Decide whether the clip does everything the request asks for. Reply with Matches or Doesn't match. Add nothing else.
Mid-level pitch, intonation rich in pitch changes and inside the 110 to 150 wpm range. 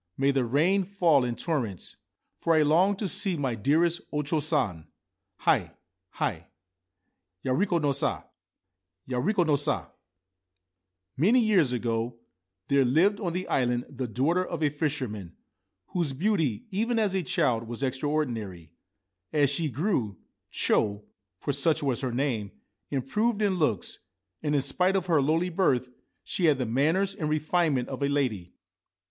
Doesn't match